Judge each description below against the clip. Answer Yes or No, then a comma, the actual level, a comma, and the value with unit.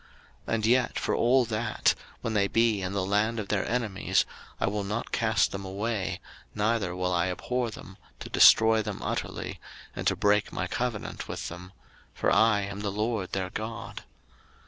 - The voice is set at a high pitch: No, low, 105 Hz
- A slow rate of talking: No, average, 180 wpm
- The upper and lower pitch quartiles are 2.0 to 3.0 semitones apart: Yes, average, 2.7 semitones